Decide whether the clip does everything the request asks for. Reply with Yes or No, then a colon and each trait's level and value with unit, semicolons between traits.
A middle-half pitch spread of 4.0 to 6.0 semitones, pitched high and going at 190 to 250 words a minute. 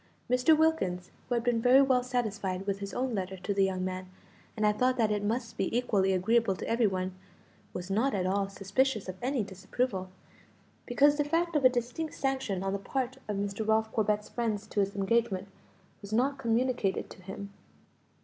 Yes: average, 4.4 semitones; high, 215 Hz; average, 195 wpm